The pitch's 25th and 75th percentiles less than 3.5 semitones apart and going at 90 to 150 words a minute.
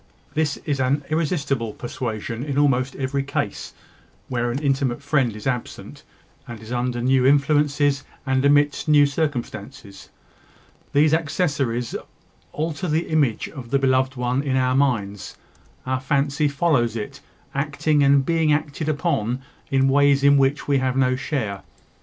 Yes: narrow, 2.5 semitones; average, 145 wpm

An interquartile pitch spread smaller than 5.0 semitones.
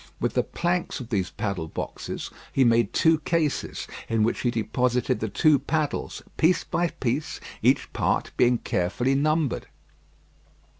No: average, 5.3 semitones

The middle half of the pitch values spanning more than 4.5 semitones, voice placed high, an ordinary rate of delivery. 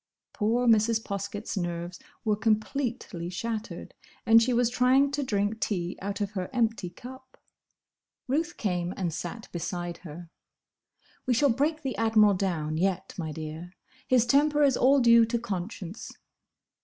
Yes: wide, 5.4 semitones; high, 220 Hz; average, 145 wpm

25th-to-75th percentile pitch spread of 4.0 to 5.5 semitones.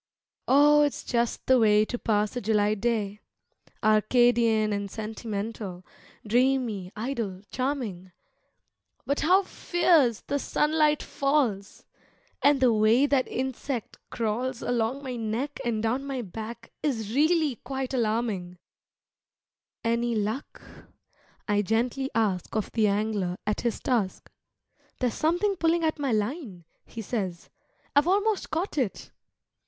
Yes: average, 4.4 semitones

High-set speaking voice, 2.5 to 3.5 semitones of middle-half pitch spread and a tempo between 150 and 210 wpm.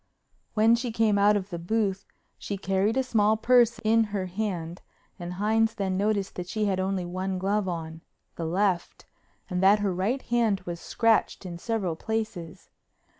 Yes: high, 200 Hz; average, 3.2 semitones; average, 165 wpm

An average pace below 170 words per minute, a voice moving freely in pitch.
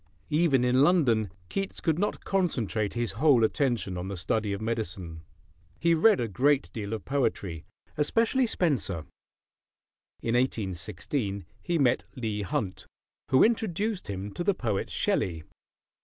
Yes: average, 140 wpm; wide, 8.0 semitones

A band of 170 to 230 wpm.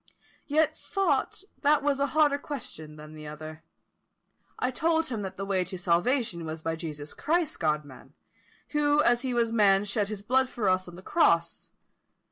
Yes: average, 185 wpm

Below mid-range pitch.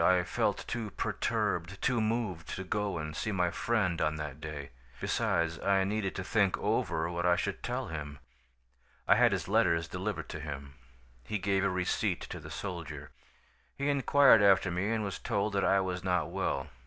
Yes: very low, 95 Hz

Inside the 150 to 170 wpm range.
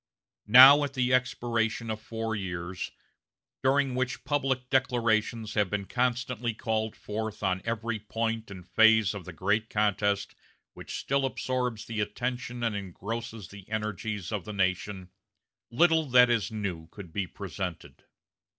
No: average, 140 wpm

